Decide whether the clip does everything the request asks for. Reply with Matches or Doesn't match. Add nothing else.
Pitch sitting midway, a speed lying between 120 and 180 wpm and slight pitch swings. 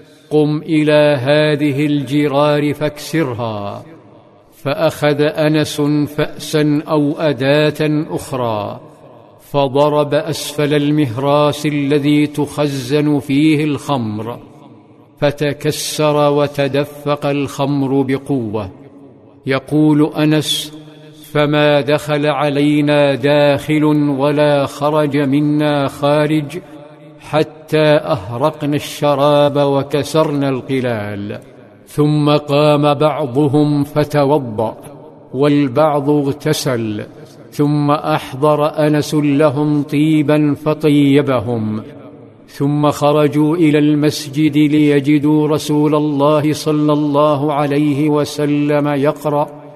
Doesn't match